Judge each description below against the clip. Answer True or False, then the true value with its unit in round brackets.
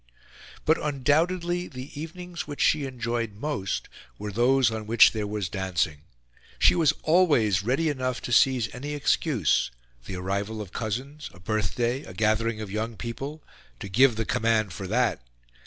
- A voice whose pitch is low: True (120 Hz)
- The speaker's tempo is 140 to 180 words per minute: True (155 wpm)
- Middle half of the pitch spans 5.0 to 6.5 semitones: True (5.3 semitones)